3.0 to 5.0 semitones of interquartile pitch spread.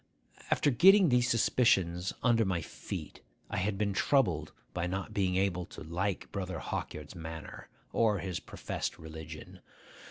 Yes: average, 4.4 semitones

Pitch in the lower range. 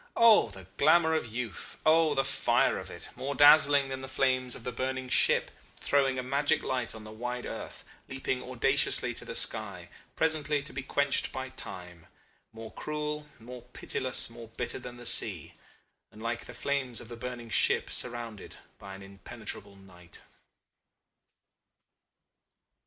Yes: low, 125 Hz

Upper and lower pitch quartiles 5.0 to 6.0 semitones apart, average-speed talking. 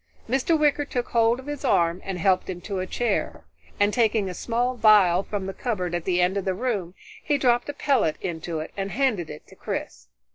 No: wide, 5.4 semitones; fast, 220 wpm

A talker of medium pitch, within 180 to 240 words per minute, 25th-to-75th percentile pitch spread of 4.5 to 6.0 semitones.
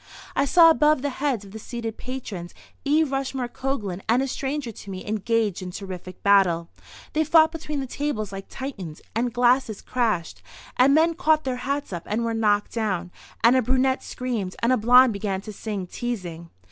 No: high, 235 Hz; average, 185 wpm; average, 5.3 semitones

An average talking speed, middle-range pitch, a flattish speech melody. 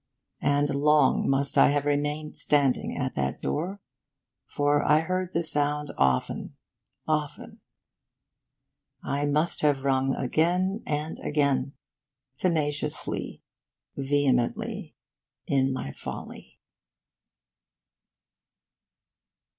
No: slow, 90 wpm; medium, 145 Hz; narrow, 1.8 semitones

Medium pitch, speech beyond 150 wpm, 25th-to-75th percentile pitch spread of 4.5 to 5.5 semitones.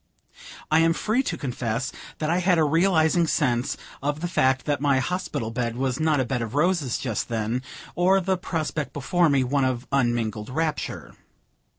Yes: medium, 145 Hz; average, 180 wpm; average, 4.8 semitones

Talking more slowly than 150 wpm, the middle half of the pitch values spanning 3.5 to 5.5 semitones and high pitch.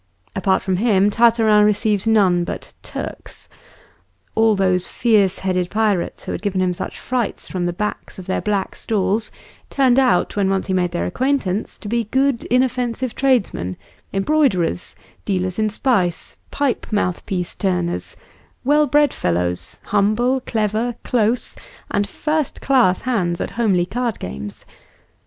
Yes: average, 140 wpm; average, 4.6 semitones; high, 210 Hz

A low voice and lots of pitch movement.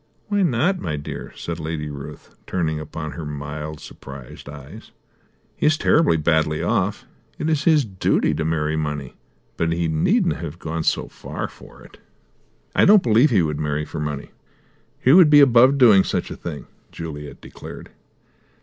Yes: very low, 80 Hz; wide, 8.9 semitones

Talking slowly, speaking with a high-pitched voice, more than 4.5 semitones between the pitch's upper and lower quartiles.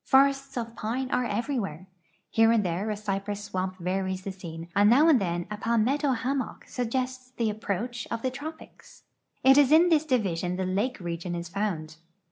No: average, 185 wpm; high, 215 Hz; wide, 5.5 semitones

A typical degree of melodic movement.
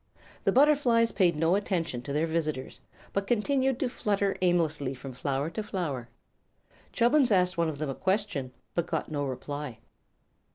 No: wide, 6.4 semitones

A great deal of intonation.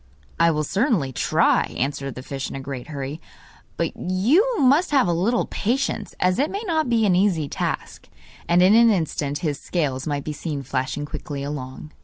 Yes: wide, 7.6 semitones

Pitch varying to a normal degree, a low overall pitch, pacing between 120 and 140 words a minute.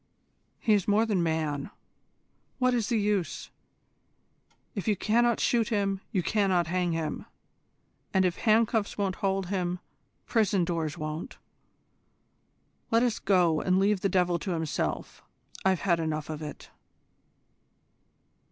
No: average, 3.7 semitones; high, 190 Hz; slow, 135 wpm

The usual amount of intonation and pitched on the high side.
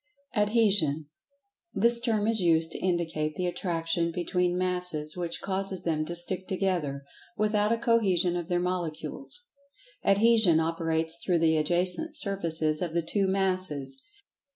No: average, 3.3 semitones; medium, 180 Hz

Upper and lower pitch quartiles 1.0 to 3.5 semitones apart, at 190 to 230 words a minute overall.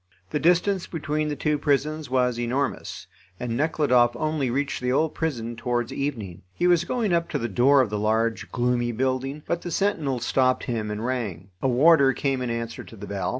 No: average, 4.3 semitones; average, 195 wpm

